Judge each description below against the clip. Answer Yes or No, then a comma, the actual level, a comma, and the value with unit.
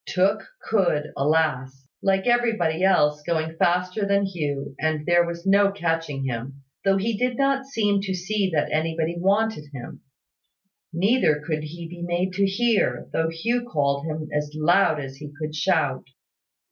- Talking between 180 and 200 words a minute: No, average, 160 wpm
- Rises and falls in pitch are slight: No, average, 4.6 semitones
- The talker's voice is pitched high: No, medium, 170 Hz